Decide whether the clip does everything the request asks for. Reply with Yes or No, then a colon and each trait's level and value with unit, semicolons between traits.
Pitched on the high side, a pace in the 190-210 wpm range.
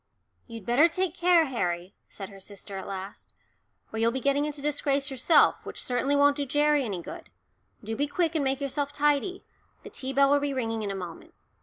Yes: very high, 275 Hz; fast, 205 wpm